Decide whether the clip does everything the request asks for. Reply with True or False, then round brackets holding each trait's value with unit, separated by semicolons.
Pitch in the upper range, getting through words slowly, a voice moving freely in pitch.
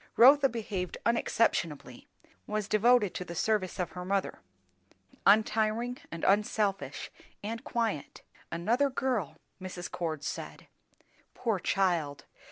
False (205 Hz; 110 wpm; 4.3 semitones)